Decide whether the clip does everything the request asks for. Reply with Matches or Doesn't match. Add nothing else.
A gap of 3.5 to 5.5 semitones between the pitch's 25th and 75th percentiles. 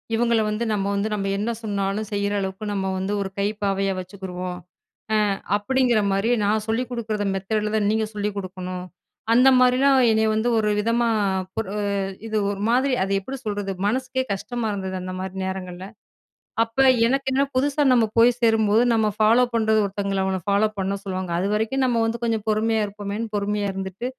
Doesn't match